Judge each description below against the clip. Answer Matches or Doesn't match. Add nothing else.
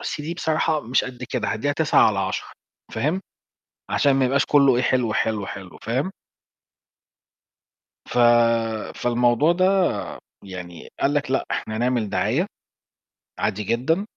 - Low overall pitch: Matches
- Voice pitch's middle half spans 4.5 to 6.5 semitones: Matches